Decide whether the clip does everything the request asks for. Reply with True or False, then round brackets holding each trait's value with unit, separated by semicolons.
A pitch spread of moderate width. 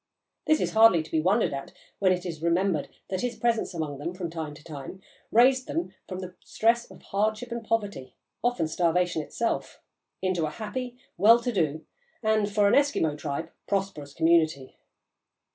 False (5.9 semitones)